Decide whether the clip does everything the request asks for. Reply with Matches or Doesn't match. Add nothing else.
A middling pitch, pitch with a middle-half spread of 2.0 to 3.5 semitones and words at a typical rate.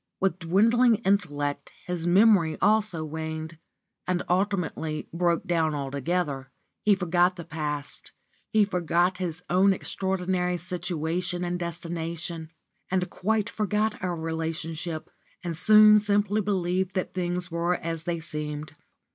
Doesn't match